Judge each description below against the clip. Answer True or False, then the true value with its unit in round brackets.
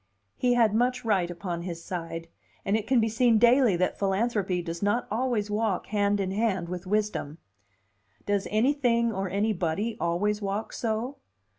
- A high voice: True (205 Hz)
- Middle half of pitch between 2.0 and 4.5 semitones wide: True (3.8 semitones)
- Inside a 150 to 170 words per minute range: True (160 wpm)